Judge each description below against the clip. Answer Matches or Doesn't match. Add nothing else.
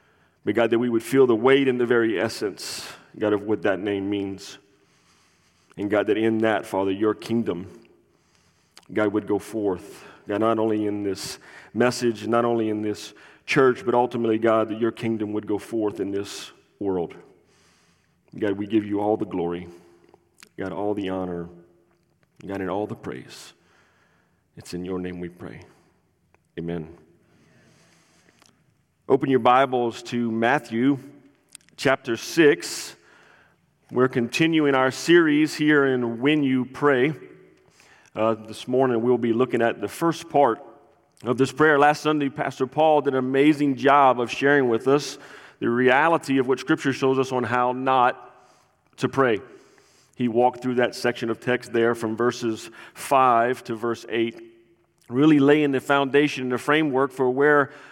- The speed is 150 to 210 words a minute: Matches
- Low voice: Matches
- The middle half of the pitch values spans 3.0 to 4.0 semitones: Doesn't match